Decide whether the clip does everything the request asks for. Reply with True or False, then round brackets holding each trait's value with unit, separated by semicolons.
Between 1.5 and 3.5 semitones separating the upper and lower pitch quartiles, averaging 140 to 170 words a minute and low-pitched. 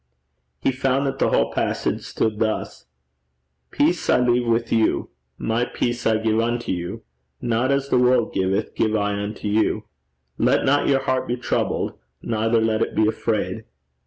True (2.6 semitones; 165 wpm; 115 Hz)